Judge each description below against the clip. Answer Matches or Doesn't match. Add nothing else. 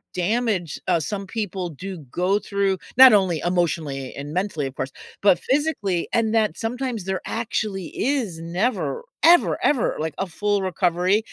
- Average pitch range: Matches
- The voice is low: Doesn't match